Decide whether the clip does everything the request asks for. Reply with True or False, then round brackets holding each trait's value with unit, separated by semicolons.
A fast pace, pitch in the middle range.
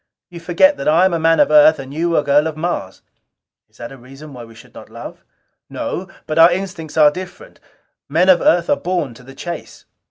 True (220 wpm; 165 Hz)